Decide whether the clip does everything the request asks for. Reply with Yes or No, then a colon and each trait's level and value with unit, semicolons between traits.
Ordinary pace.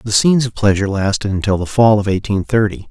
No: fast, 225 wpm